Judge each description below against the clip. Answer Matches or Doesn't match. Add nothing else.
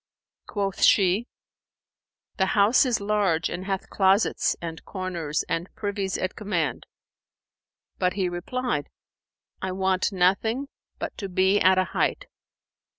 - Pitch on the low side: Doesn't match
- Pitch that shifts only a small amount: Matches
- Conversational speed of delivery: Doesn't match